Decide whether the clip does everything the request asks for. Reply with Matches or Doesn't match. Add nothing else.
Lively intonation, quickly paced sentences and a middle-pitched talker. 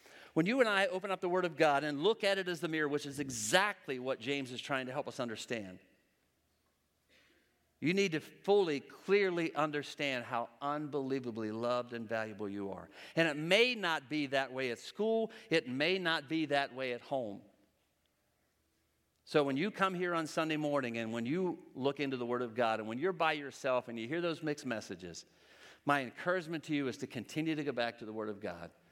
Matches